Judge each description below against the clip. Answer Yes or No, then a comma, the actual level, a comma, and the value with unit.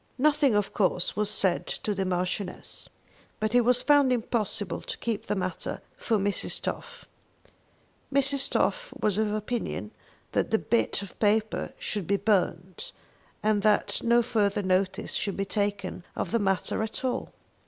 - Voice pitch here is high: Yes, high, 210 Hz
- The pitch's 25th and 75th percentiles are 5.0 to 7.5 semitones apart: No, average, 3.4 semitones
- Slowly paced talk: No, average, 155 wpm